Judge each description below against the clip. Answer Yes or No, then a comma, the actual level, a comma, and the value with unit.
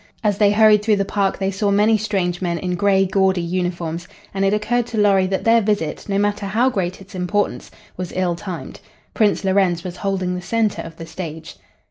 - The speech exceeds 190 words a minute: Yes, fast, 205 wpm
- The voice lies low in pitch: No, high, 195 Hz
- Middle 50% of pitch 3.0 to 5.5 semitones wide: No, narrow, 2.5 semitones